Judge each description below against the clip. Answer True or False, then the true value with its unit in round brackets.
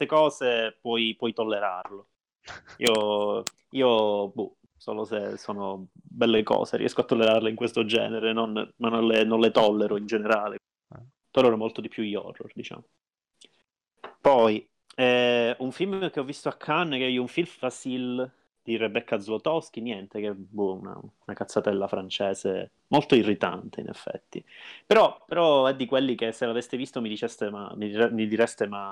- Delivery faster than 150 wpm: True (165 wpm)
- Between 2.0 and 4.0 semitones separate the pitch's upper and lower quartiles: True (3.1 semitones)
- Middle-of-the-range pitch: False (115 Hz)